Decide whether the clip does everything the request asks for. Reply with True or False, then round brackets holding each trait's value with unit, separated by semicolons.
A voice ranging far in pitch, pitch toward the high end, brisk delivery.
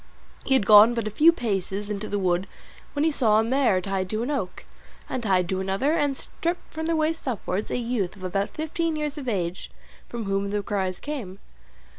True (6.7 semitones; 215 Hz; 210 wpm)